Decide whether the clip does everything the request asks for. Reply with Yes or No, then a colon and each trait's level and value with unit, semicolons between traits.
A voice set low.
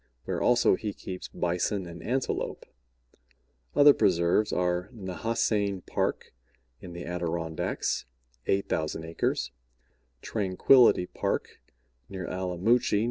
Yes: very low, 95 Hz